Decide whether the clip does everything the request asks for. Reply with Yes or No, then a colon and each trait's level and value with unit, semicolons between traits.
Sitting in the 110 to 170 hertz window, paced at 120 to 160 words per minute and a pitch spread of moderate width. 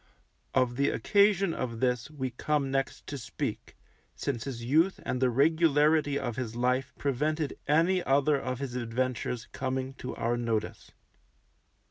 Yes: low, 135 Hz; average, 145 wpm; average, 3.3 semitones